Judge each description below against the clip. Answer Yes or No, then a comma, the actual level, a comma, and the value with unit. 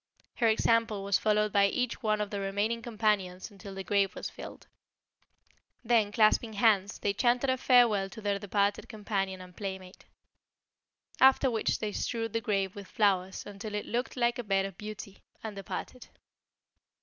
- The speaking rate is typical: Yes, average, 165 wpm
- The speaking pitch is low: No, high, 210 Hz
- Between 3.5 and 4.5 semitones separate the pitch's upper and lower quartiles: No, narrow, 2.5 semitones